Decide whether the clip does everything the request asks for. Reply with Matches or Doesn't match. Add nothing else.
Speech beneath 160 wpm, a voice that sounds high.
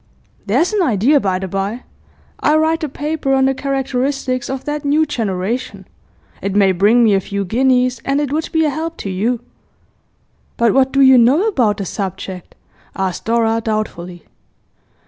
Doesn't match